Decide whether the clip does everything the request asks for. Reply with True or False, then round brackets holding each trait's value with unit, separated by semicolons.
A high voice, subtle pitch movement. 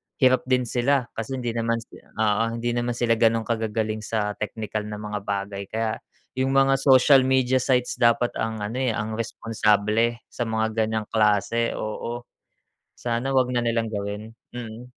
False (115 Hz; 2.2 semitones)